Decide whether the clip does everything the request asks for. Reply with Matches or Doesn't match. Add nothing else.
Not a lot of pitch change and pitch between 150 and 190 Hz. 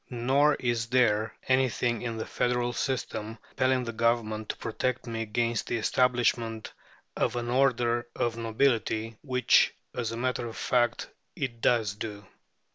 Doesn't match